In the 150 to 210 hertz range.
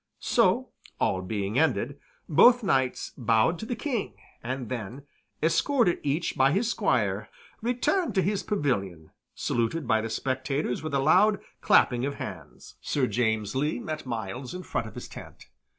No: low, 135 Hz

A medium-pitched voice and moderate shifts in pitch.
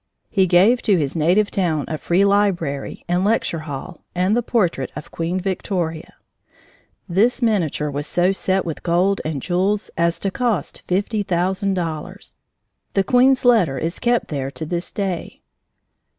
Yes: medium, 180 Hz; average, 3.7 semitones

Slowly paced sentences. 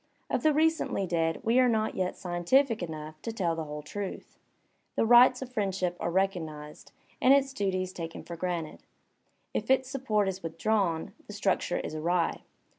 No: average, 170 wpm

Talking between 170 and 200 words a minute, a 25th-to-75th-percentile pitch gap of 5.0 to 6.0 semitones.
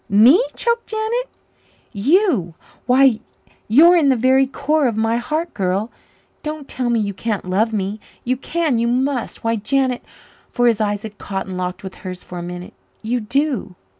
Yes: average, 175 wpm; wide, 5.5 semitones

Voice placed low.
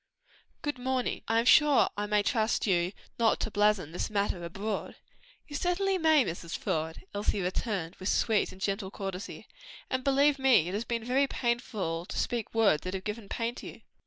No: high, 215 Hz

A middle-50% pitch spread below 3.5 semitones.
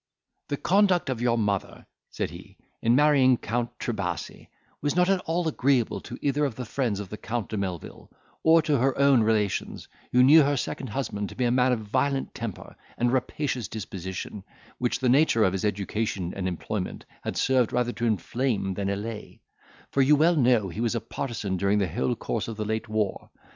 No: average, 4.7 semitones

